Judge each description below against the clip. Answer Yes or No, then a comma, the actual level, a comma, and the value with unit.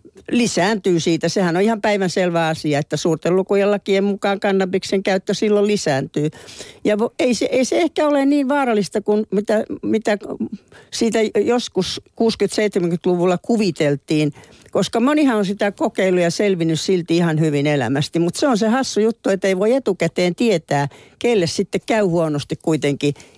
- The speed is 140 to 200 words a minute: Yes, average, 150 wpm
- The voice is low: No, high, 195 Hz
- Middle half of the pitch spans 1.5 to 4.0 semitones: No, average, 4.5 semitones